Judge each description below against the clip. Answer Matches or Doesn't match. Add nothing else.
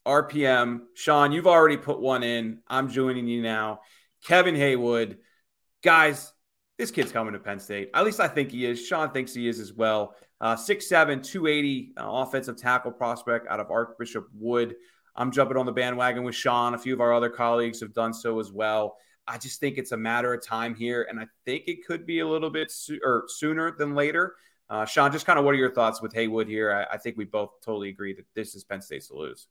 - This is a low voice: Matches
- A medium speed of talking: Doesn't match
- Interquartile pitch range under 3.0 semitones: Doesn't match